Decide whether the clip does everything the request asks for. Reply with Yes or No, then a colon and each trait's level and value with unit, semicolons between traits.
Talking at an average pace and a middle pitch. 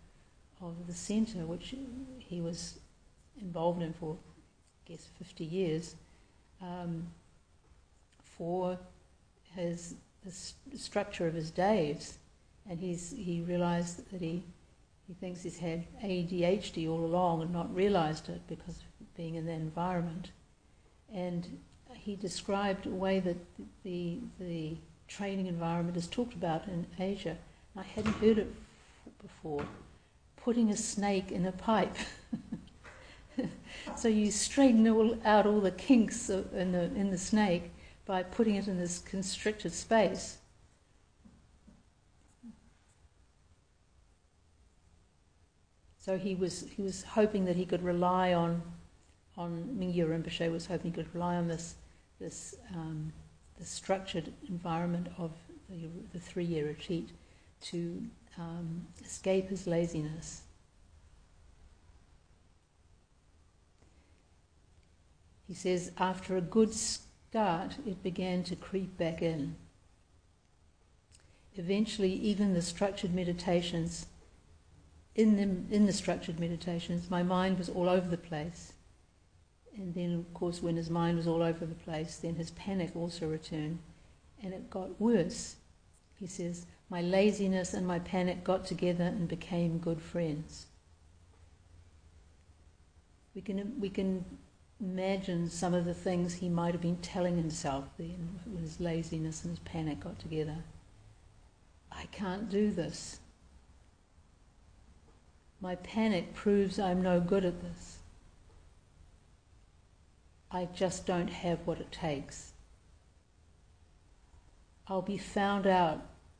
No: slow, 125 wpm; medium, 170 Hz